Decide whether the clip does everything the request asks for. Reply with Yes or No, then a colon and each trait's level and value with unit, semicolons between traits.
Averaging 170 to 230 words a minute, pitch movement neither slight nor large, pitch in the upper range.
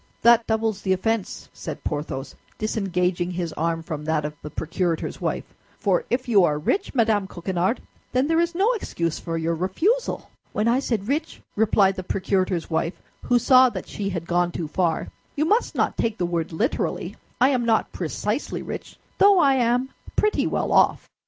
No: average, 180 wpm; wide, 6.5 semitones; high, 195 Hz